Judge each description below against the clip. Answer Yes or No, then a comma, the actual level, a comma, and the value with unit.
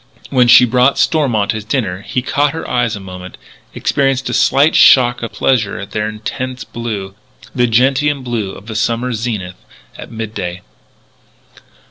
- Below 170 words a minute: Yes, average, 155 wpm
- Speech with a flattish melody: No, average, 3.4 semitones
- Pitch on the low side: Yes, low, 120 Hz